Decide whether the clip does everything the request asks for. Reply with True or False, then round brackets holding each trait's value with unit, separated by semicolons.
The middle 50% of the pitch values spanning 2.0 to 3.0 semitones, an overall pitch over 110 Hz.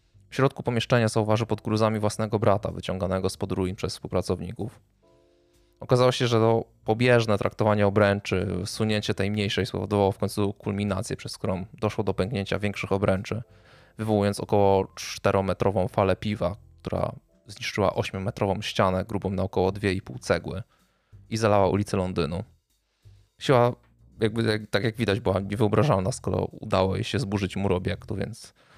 False (2.5 semitones; 100 Hz)